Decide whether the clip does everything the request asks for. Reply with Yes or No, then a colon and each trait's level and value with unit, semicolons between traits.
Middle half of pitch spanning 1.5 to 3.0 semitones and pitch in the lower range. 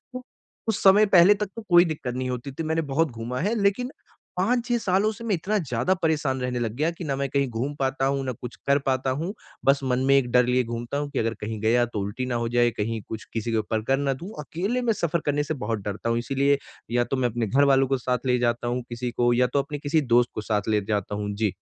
No: average, 5.0 semitones; low, 130 Hz